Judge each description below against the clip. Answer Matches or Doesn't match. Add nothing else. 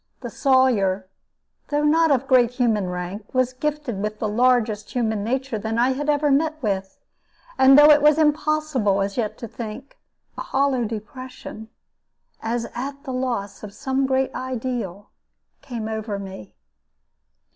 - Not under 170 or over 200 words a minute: Doesn't match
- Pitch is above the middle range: Matches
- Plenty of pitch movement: Doesn't match